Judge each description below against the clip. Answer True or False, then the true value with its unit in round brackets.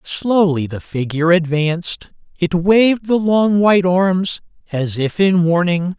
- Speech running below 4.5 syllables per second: True (4.1 syllables/s)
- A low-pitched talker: False (175 Hz)